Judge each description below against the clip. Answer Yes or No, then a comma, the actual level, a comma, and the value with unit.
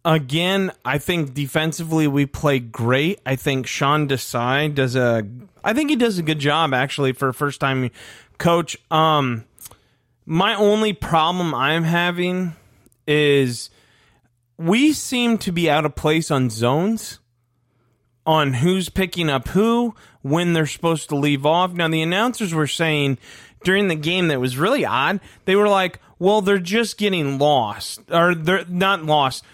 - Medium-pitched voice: Yes, medium, 155 Hz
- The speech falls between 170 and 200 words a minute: No, average, 155 wpm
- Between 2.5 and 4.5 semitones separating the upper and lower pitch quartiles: No, wide, 5.5 semitones